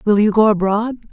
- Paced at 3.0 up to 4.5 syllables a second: No, 5.1 syllables/s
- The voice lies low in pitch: No, high, 210 Hz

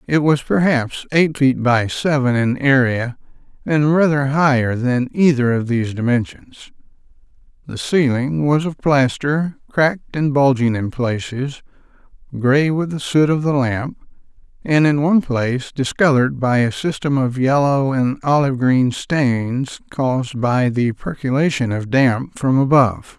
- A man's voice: Yes, male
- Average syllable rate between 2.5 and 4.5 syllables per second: Yes, 4.3 syllables/s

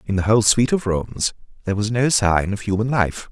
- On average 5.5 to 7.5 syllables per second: Yes, 5.9 syllables/s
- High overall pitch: No, low, 105 Hz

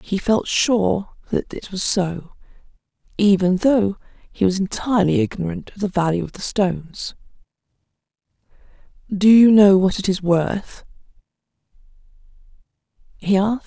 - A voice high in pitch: Yes, high, 195 Hz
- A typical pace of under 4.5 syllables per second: No, 4.6 syllables/s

